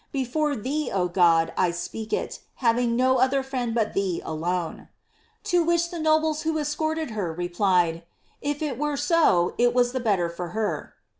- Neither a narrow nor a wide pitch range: No, wide, 8.8 semitones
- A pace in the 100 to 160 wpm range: No, average, 180 wpm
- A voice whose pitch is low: No, high, 240 Hz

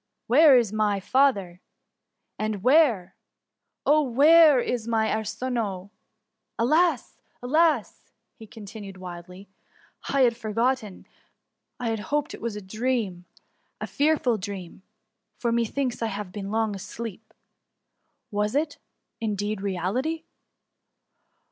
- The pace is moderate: No, slow, 110 wpm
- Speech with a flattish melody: No, average, 4.4 semitones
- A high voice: Yes, high, 225 Hz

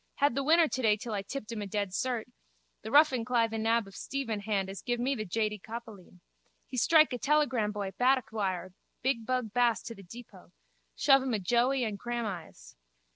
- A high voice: Yes, high, 230 Hz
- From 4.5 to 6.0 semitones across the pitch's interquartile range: No, average, 3.6 semitones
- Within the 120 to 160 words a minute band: No, average, 195 wpm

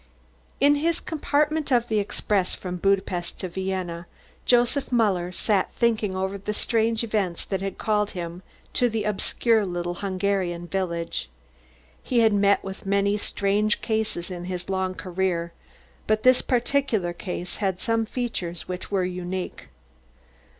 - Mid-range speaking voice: No, high, 195 Hz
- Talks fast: No, average, 145 wpm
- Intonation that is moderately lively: Yes, average, 3.6 semitones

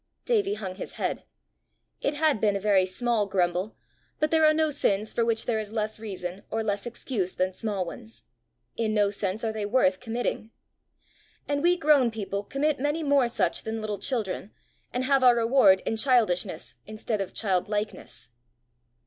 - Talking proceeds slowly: No, average, 175 wpm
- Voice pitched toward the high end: Yes, high, 220 Hz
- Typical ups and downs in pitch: Yes, average, 4.4 semitones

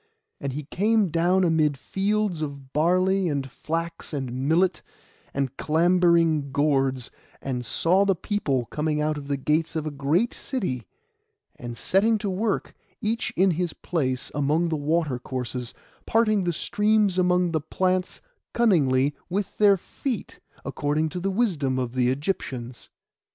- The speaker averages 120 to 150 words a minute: Yes, average, 145 wpm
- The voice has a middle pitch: Yes, medium, 160 Hz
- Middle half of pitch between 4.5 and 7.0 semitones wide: Yes, average, 5.2 semitones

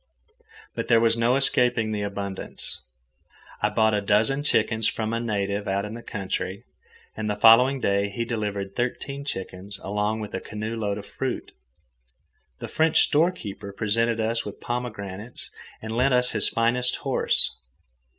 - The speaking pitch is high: No, low, 110 Hz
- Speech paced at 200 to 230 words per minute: No, average, 155 wpm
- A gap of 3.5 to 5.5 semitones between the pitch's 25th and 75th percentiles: No, average, 2.8 semitones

